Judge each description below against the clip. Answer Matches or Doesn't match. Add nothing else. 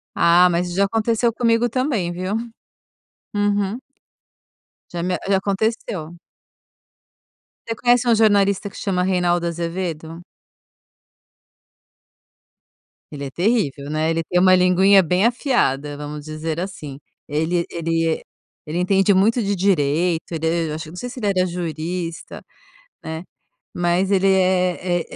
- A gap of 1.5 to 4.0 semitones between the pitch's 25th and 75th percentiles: Matches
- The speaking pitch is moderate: Matches